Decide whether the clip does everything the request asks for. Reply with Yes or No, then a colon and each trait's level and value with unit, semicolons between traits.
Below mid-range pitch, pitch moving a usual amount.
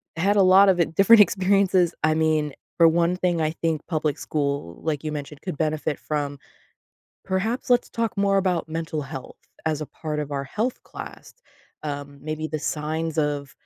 No: medium, 160 Hz; average, 3.7 semitones